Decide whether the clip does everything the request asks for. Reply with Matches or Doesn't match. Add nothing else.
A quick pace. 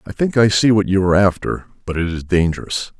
Matches